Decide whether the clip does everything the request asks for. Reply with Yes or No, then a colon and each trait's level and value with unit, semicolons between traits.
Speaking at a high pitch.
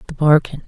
No: medium, 150 Hz